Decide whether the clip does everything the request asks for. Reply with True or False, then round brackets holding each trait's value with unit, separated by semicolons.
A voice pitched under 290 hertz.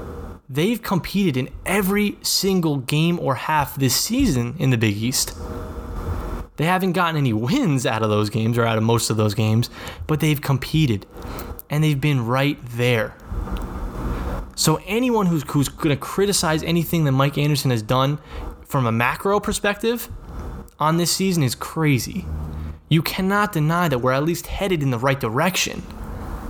True (140 Hz)